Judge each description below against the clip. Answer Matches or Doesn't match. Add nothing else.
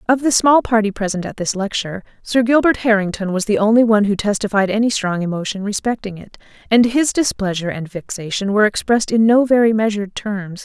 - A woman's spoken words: Matches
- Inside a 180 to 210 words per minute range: Matches